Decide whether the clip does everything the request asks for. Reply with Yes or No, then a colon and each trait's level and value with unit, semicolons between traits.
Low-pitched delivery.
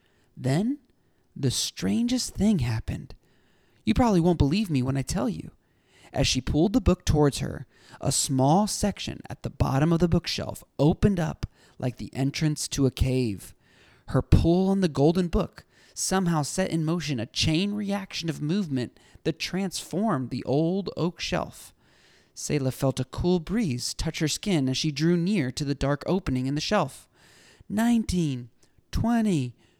No: medium, 155 Hz